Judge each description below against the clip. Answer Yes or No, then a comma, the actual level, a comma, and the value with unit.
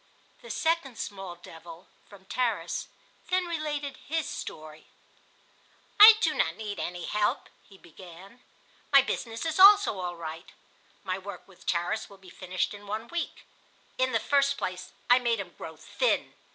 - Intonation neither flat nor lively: No, wide, 7.6 semitones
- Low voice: No, high, 205 Hz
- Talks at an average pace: Yes, average, 155 wpm